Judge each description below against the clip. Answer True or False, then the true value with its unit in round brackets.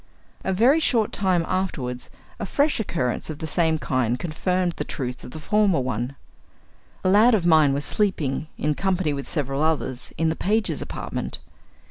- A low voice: False (160 Hz)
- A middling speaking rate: True (170 wpm)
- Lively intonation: True (5.7 semitones)